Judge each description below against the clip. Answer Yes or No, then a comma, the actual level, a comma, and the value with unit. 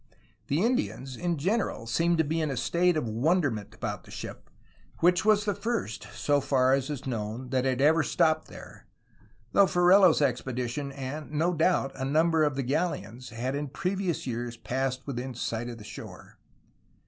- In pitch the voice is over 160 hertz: No, medium, 140 Hz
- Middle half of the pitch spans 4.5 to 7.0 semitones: Yes, average, 5.2 semitones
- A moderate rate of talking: Yes, average, 175 wpm